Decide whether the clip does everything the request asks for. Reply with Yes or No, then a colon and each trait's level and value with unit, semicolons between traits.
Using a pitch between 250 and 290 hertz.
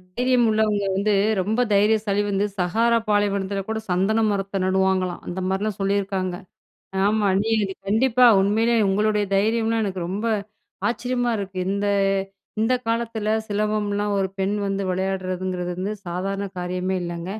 No: high, 200 Hz